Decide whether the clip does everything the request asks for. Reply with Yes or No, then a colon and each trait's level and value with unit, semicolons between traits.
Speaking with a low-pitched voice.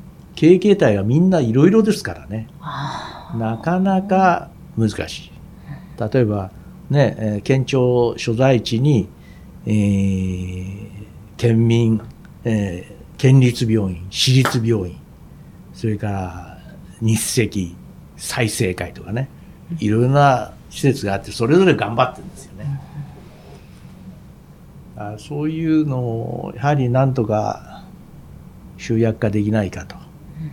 Yes: low, 115 Hz